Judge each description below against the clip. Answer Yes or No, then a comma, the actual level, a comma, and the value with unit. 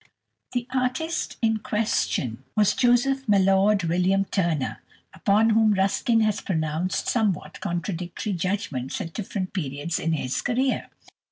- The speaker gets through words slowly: Yes, slow, 120 wpm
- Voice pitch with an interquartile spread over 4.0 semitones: Yes, average, 4.7 semitones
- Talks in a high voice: Yes, high, 195 Hz